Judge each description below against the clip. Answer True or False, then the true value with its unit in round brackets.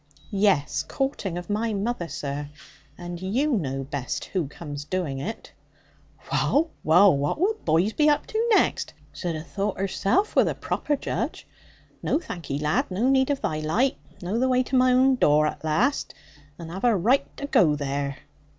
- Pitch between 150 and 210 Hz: True (190 Hz)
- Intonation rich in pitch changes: True (8.9 semitones)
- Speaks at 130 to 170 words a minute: False (180 wpm)